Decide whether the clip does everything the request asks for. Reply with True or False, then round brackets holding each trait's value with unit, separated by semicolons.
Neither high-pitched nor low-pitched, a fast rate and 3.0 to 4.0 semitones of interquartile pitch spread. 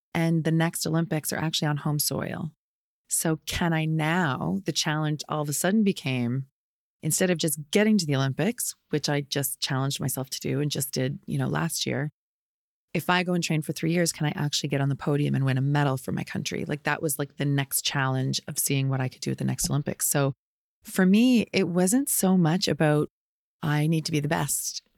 True (150 Hz; 225 wpm; 3.3 semitones)